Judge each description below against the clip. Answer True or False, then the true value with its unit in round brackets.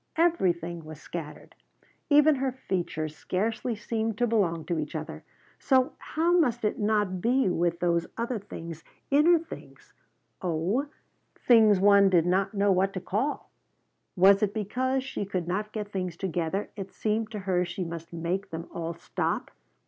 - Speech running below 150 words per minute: False (160 wpm)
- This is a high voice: True (195 Hz)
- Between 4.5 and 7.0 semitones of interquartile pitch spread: True (4.8 semitones)